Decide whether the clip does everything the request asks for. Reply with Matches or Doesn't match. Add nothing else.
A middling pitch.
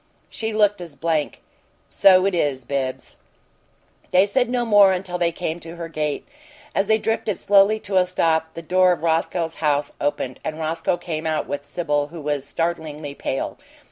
Matches